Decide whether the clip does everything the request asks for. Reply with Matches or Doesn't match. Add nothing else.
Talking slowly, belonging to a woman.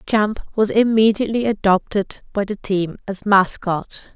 Matches